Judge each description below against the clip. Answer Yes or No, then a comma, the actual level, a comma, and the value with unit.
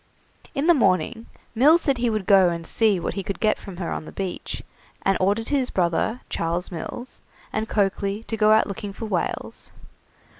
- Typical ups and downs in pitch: Yes, average, 3.5 semitones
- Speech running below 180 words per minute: No, average, 190 wpm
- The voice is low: No, high, 205 Hz